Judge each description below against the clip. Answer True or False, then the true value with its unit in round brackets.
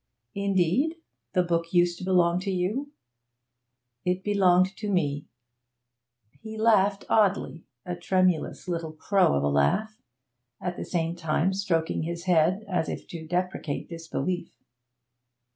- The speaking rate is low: True (130 wpm)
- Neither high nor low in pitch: True (180 Hz)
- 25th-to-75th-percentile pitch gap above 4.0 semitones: False (2.8 semitones)